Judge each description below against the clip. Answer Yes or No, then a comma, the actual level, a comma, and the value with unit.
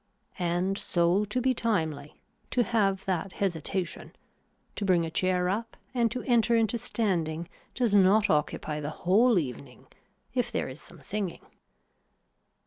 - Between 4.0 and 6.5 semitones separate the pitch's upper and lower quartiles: Yes, average, 4.9 semitones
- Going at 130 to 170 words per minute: Yes, average, 140 wpm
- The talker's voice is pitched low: No, high, 190 Hz